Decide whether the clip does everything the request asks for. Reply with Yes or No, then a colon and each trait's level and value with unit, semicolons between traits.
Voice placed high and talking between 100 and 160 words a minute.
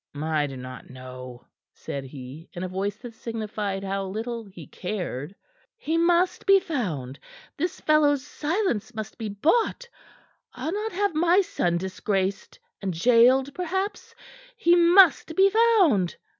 Yes: high, 225 Hz; average, 140 wpm